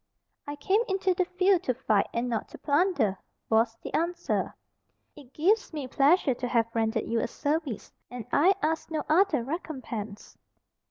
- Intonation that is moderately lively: No, wide, 6.9 semitones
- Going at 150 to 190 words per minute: Yes, average, 165 wpm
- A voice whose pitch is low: No, very high, 285 Hz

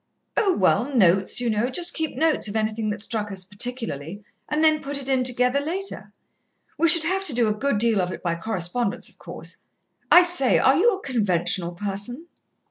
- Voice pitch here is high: Yes, high, 240 Hz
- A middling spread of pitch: No, wide, 6.8 semitones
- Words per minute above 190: Yes, average, 200 wpm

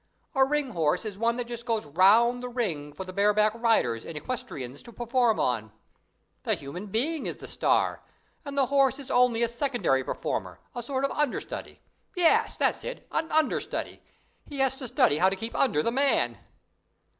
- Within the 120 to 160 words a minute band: No, average, 185 wpm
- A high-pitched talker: Yes, high, 235 Hz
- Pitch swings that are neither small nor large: No, wide, 5.9 semitones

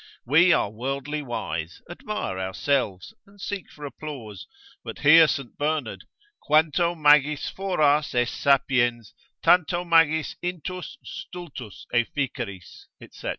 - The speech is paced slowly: Yes, slow, 110 wpm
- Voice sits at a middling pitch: Yes, medium, 145 Hz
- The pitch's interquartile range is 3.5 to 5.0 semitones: No, wide, 5.4 semitones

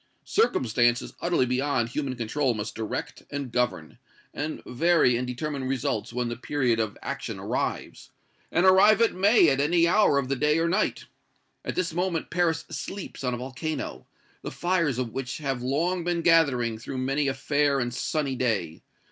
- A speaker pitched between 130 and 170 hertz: Yes, medium, 140 Hz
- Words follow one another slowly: No, average, 175 wpm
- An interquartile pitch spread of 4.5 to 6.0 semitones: Yes, average, 5.1 semitones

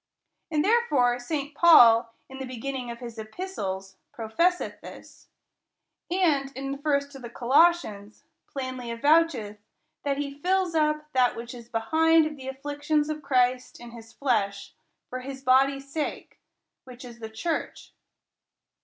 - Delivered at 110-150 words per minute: Yes, average, 145 wpm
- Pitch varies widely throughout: No, average, 4.2 semitones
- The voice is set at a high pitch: Yes, very high, 270 Hz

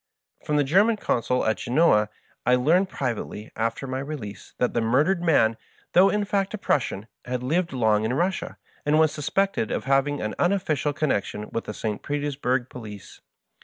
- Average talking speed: Yes, average, 175 wpm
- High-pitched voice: No, low, 135 Hz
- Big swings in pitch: Yes, wide, 6.5 semitones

